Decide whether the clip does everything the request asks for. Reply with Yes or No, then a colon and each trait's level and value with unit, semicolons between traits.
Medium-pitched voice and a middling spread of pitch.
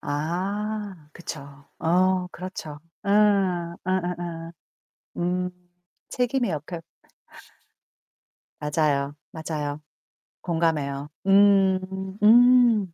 Yes: medium, 175 Hz; average, 4.1 semitones